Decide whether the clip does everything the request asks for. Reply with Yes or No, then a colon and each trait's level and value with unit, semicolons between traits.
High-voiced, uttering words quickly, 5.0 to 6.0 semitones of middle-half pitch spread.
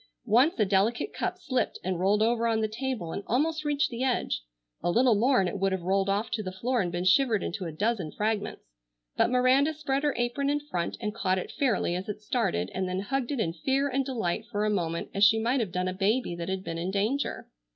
Yes: high, 215 Hz; fast, 245 wpm; average, 5.3 semitones